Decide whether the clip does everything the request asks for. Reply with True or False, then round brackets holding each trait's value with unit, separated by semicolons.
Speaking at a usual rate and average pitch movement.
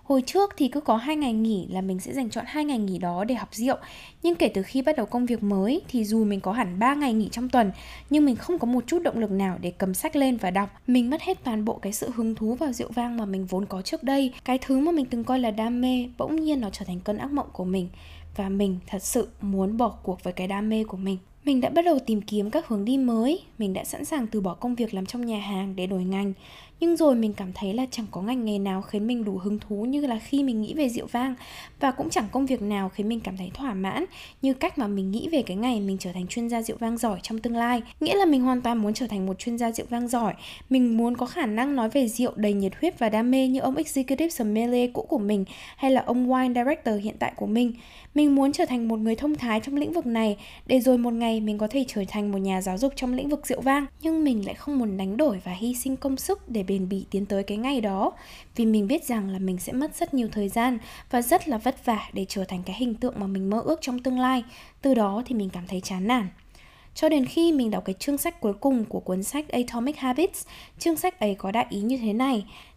False (280 wpm; 4.8 semitones)